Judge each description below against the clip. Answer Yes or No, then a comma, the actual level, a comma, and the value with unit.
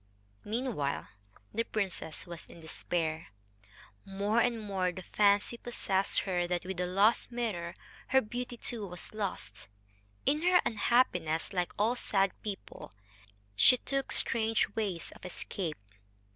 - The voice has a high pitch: Yes, high, 200 Hz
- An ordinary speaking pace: No, slow, 130 wpm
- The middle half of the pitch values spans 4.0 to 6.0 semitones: Yes, average, 4.7 semitones